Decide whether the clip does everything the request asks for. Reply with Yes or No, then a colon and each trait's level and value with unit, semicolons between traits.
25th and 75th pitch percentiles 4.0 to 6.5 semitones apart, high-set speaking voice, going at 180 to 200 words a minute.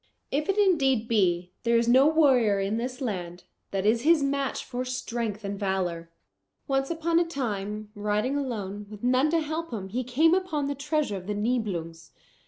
Yes: wide, 5.6 semitones; high, 240 Hz; average, 185 wpm